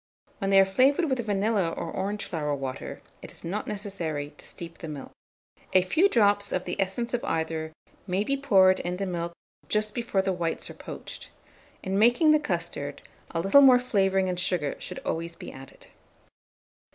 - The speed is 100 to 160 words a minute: No, average, 185 wpm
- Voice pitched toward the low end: No, high, 190 Hz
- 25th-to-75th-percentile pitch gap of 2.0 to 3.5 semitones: No, average, 4.1 semitones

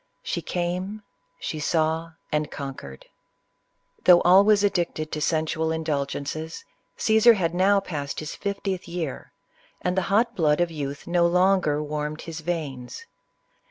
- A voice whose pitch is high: No, medium, 165 Hz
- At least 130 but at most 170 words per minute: Yes, average, 140 wpm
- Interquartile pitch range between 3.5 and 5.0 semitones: Yes, average, 3.8 semitones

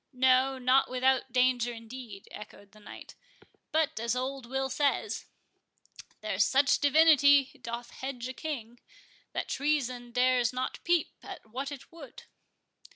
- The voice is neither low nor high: No, very high, 255 Hz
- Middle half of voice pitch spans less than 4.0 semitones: Yes, narrow, 2.6 semitones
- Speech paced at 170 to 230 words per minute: No, slow, 135 wpm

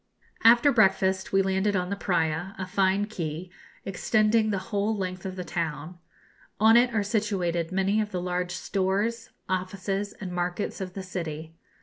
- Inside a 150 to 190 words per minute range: Yes, average, 165 wpm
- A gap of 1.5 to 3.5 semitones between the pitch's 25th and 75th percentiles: Yes, narrow, 2.4 semitones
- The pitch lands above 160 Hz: Yes, high, 190 Hz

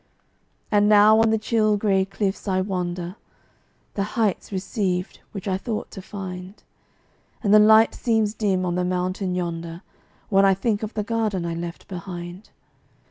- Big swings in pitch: No, average, 2.8 semitones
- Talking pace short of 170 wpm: Yes, average, 160 wpm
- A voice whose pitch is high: Yes, high, 195 Hz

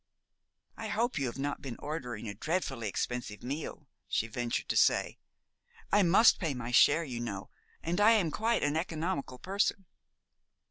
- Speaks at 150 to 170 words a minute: Yes, average, 160 wpm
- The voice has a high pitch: No, medium, 145 Hz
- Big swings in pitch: Yes, wide, 7.2 semitones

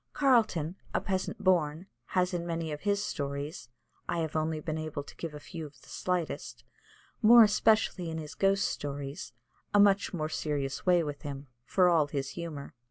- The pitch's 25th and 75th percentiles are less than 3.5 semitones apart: No, average, 4.1 semitones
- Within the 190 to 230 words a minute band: No, average, 180 wpm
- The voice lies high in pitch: No, medium, 165 Hz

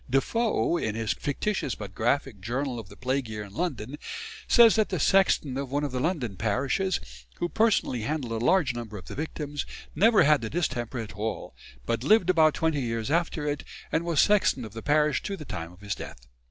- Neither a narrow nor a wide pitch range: No, wide, 6.6 semitones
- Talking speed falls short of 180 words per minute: No, fast, 205 wpm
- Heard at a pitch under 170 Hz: Yes, medium, 140 Hz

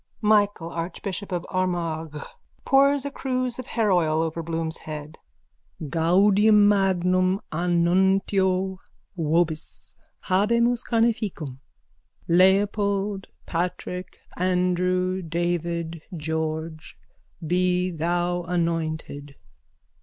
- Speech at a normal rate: No, slow, 80 wpm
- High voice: No, medium, 180 Hz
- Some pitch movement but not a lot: Yes, average, 3.0 semitones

